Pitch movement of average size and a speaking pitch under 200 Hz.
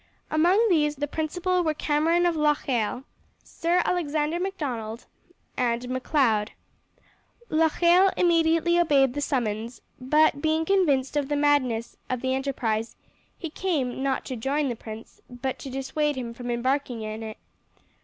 No: average, 4.6 semitones; very high, 285 Hz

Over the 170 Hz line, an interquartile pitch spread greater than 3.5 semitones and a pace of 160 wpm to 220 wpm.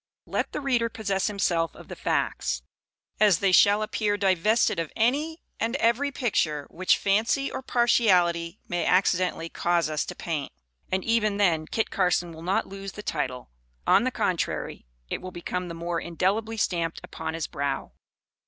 Yes: high, 190 Hz; average, 4.6 semitones; average, 165 wpm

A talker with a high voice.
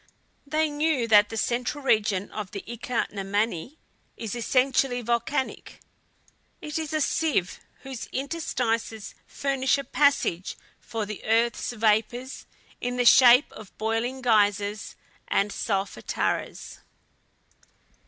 Yes: high, 235 Hz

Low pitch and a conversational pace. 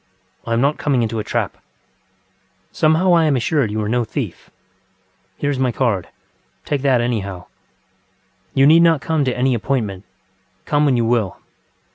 Yes: low, 125 Hz; average, 165 wpm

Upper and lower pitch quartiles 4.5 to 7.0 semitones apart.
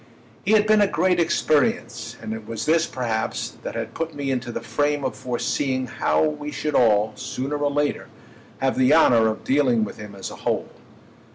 Yes: average, 4.9 semitones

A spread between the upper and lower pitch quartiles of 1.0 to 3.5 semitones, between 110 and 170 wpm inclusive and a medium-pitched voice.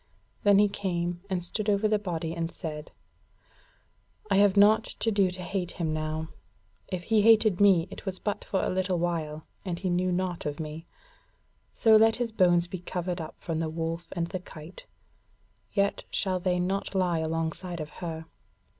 No: average, 3.1 semitones; average, 180 wpm; medium, 180 Hz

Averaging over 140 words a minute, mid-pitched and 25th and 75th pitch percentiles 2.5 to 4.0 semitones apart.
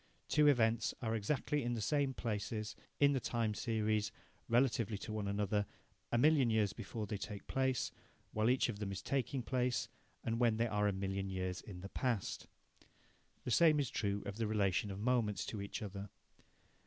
No: average, 185 wpm; low, 110 Hz; average, 3.4 semitones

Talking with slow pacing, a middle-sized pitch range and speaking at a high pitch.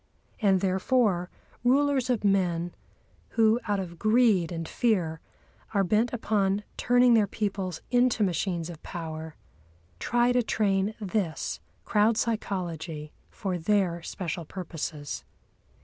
Yes: slow, 115 wpm; average, 4.5 semitones; high, 195 Hz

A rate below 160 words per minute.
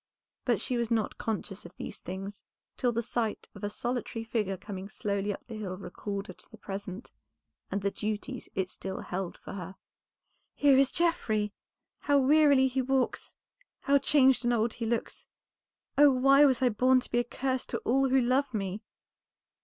No: average, 185 wpm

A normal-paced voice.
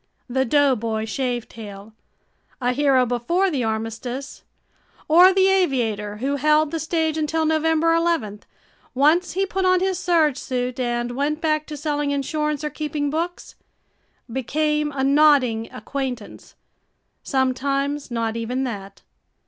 No: slow, 130 wpm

